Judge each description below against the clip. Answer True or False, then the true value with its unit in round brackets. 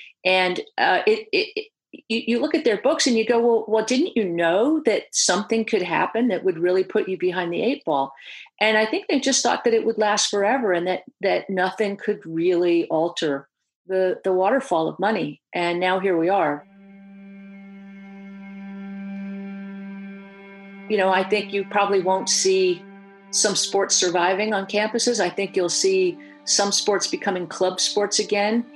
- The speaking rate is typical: True (175 wpm)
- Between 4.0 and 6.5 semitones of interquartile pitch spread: False (3.1 semitones)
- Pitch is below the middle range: False (195 Hz)